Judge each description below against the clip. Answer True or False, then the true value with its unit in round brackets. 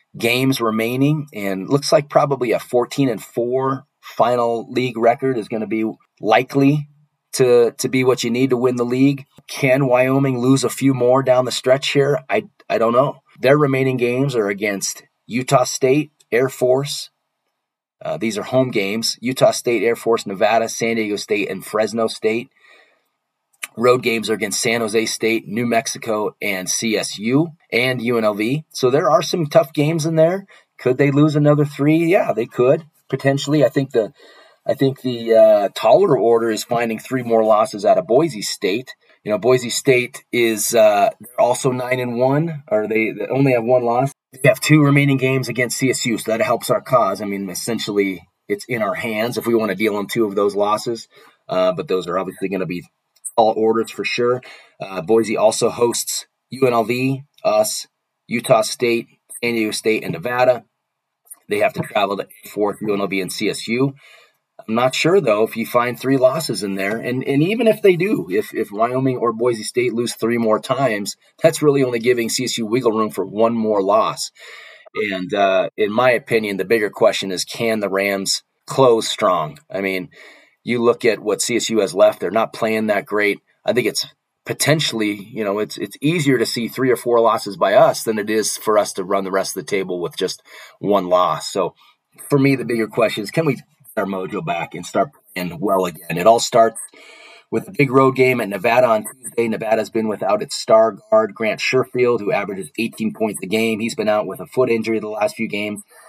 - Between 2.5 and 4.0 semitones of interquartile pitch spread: True (3.6 semitones)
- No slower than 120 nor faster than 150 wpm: False (195 wpm)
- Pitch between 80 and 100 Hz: False (120 Hz)